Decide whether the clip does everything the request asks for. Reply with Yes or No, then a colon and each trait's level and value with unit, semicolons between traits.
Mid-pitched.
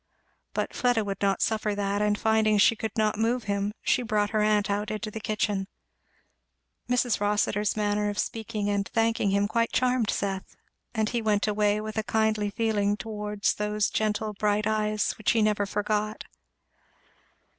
No: high, 210 Hz